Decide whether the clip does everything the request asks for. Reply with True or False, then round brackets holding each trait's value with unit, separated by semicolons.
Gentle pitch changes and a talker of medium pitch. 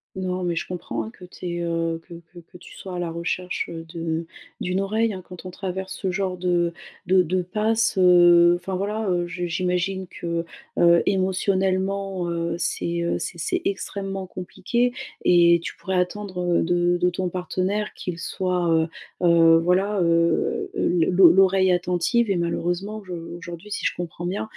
True (1.8 semitones; 180 Hz)